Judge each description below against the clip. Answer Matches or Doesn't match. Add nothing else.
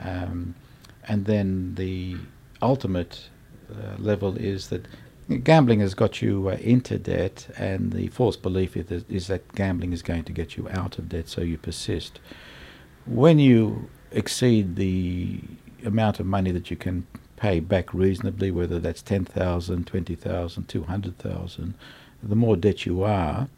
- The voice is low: Matches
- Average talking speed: Matches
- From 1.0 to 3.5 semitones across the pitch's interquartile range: Doesn't match